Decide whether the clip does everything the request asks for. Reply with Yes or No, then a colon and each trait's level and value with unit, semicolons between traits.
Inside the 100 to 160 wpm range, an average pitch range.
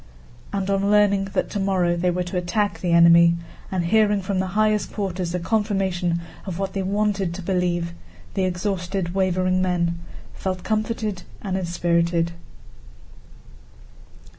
No: average, 140 wpm; narrow, 2.3 semitones